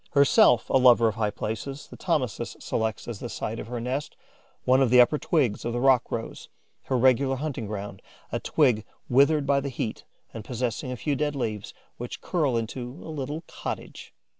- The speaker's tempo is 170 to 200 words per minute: Yes, average, 190 wpm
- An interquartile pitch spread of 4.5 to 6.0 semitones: No, average, 3.4 semitones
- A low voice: Yes, low, 125 Hz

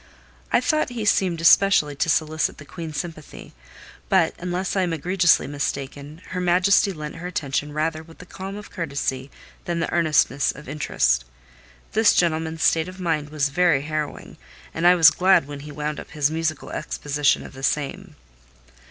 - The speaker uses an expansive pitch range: No, average, 3.4 semitones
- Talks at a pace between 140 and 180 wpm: Yes, average, 170 wpm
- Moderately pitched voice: Yes, medium, 160 Hz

